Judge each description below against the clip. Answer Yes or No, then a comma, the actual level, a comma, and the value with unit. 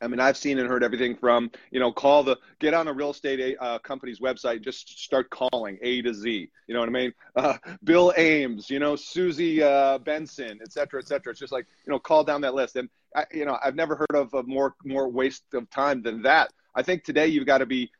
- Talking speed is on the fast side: Yes, fast, 250 wpm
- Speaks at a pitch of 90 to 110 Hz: No, low, 135 Hz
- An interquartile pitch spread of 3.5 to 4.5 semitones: No, average, 3.0 semitones